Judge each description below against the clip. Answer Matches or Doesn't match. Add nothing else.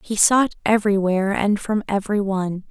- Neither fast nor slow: Matches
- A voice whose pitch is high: Matches